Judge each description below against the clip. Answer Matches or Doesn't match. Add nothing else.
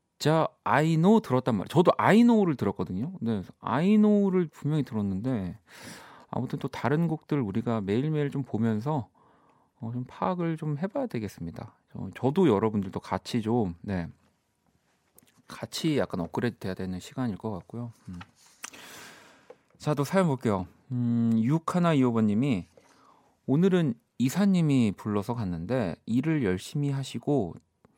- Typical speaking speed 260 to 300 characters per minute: Matches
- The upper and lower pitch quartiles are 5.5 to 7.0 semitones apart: Matches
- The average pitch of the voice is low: Matches